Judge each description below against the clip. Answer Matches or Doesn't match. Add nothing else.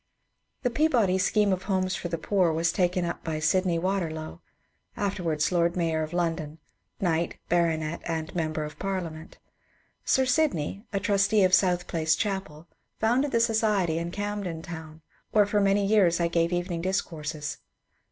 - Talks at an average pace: Matches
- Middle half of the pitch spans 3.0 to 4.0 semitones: Matches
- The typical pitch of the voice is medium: Matches